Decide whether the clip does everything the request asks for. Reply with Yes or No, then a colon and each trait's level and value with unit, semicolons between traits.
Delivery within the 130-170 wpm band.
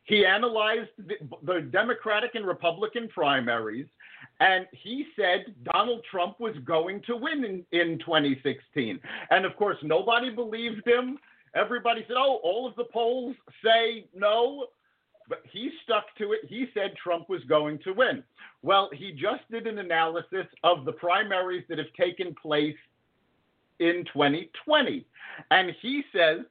Yes: average, 145 wpm